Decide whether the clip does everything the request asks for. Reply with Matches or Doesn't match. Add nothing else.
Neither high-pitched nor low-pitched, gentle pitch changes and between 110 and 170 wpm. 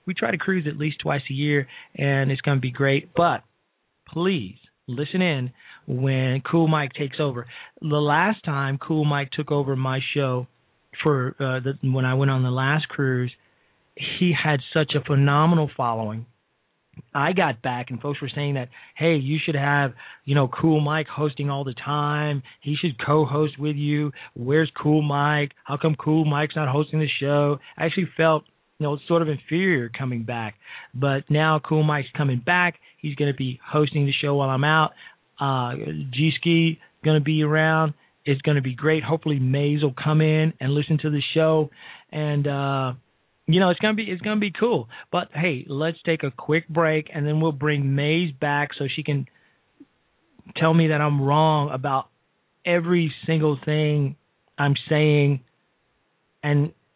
Doesn't match